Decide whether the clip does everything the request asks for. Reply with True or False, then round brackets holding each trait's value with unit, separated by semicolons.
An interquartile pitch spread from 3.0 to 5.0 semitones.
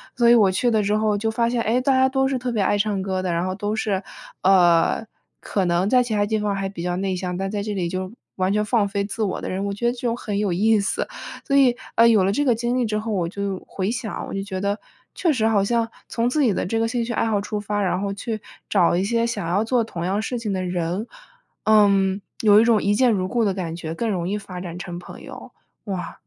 True (3.3 semitones)